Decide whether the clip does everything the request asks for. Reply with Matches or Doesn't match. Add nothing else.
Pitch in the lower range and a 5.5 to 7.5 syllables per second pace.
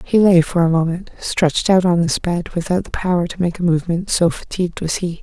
Doesn't match